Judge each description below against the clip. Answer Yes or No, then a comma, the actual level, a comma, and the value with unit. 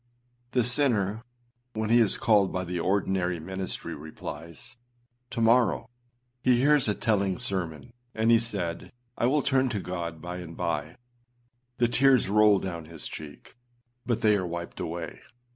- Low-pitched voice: Yes, low, 100 Hz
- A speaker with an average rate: Yes, average, 160 wpm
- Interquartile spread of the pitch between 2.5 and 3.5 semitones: No, average, 5.3 semitones